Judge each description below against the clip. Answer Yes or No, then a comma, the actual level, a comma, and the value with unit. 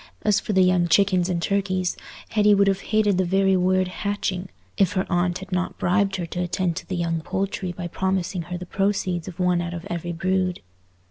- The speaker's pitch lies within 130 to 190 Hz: Yes, medium, 185 Hz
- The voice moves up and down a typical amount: No, narrow, 1.7 semitones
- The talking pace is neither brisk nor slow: No, fast, 210 wpm